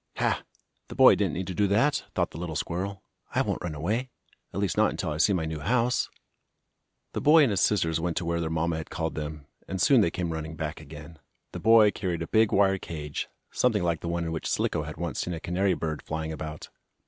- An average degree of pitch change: Yes, average, 3.8 semitones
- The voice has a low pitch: Yes, very low, 85 Hz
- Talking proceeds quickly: Yes, fast, 235 wpm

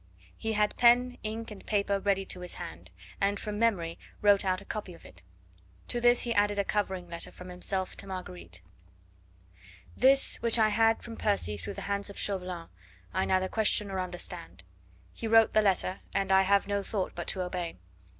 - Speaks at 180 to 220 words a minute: Yes, average, 190 wpm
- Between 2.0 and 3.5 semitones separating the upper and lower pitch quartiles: Yes, average, 2.8 semitones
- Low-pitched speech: No, high, 200 Hz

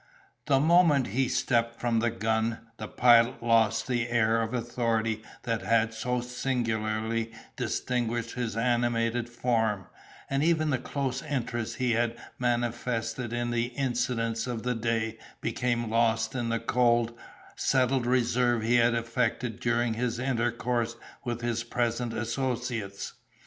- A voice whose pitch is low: Yes, low, 120 Hz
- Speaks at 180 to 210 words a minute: No, slow, 135 wpm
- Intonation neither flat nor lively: No, narrow, 1.5 semitones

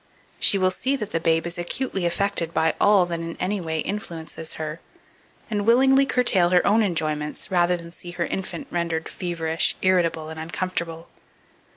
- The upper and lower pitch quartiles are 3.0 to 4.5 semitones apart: Yes, average, 3.3 semitones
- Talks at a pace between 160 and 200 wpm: Yes, average, 170 wpm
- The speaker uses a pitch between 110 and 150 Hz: No, medium, 175 Hz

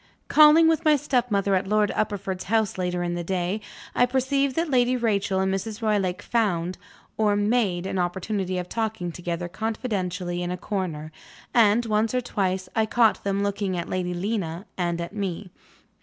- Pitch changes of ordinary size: Yes, average, 3.8 semitones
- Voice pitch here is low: No, high, 200 Hz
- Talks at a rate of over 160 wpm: Yes, average, 170 wpm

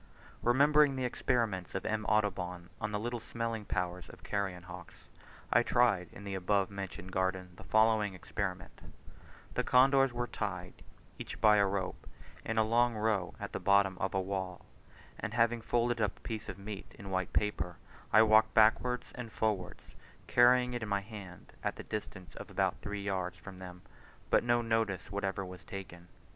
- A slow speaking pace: No, average, 180 wpm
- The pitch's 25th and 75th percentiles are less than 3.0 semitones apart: No, average, 3.4 semitones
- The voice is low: Yes, low, 100 Hz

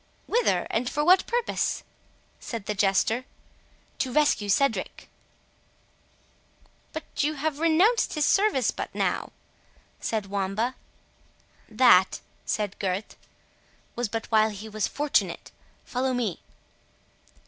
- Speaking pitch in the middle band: No, high, 240 Hz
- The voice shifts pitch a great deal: Yes, wide, 6.2 semitones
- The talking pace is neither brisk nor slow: No, slow, 105 wpm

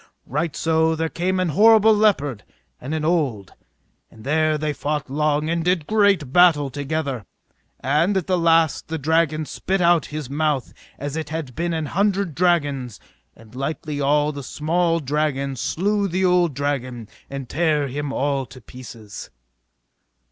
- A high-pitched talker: No, medium, 155 Hz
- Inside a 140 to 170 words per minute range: Yes, average, 160 wpm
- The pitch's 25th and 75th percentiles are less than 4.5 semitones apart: Yes, average, 3.5 semitones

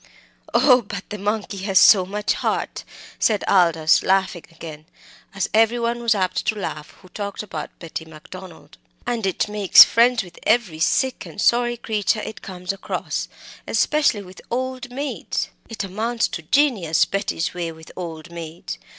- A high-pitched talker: Yes, high, 200 Hz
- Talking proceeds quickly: No, average, 160 wpm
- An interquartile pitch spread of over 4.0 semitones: Yes, average, 4.8 semitones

